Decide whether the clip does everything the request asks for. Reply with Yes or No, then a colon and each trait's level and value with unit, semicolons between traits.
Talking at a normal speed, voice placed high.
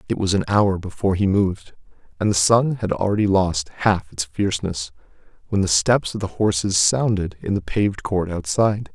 No: average, 190 wpm; very low, 95 Hz